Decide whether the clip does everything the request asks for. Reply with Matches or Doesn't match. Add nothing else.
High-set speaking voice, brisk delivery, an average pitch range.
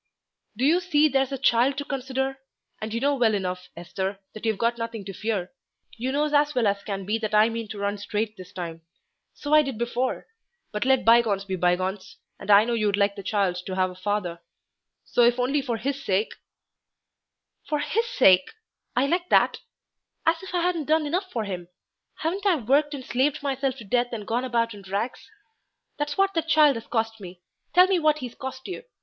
Doesn't match